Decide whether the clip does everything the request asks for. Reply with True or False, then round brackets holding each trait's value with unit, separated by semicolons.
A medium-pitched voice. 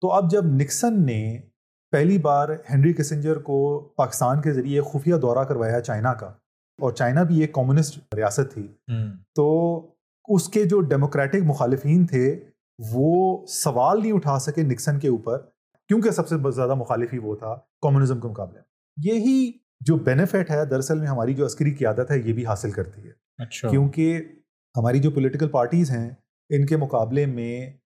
True (145 Hz)